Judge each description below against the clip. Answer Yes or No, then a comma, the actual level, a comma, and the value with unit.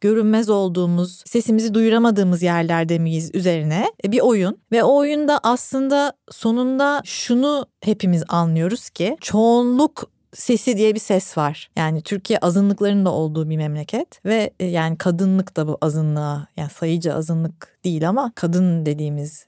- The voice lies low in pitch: No, medium, 185 Hz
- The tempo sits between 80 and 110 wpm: No, average, 135 wpm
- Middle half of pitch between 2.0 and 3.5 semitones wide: No, wide, 5.6 semitones